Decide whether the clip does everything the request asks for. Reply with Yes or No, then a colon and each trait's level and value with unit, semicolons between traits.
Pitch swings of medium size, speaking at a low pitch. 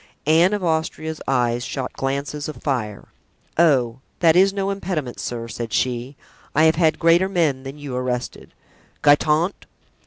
No: average, 4.8 semitones; medium, 150 Hz